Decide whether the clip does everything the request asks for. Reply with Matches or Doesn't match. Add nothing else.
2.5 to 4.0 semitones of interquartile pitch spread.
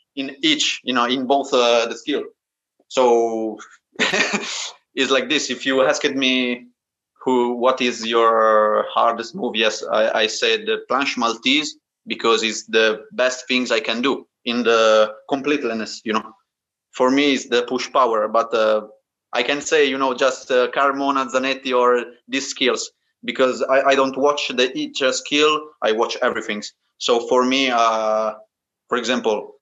Matches